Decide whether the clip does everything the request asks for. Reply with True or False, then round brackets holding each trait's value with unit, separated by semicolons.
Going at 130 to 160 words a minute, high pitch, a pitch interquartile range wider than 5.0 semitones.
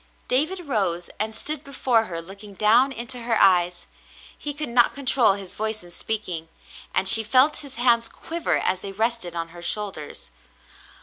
False (175 wpm; 220 Hz; 5.4 semitones)